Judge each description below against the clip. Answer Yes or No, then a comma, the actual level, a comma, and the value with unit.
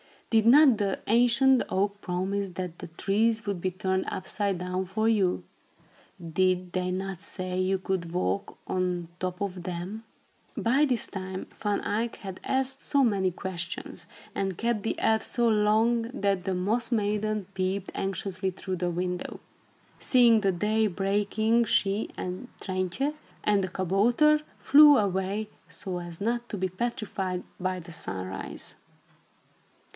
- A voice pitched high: Yes, high, 195 Hz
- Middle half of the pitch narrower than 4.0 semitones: Yes, average, 3.2 semitones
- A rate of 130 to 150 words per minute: Yes, average, 145 wpm